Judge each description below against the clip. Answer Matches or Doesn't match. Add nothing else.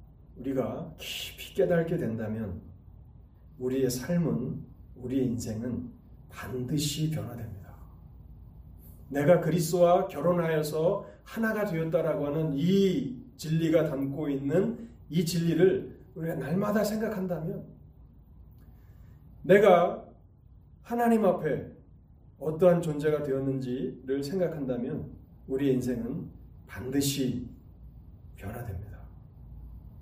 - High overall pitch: Doesn't match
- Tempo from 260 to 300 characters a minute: Doesn't match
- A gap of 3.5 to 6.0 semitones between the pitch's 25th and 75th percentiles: Doesn't match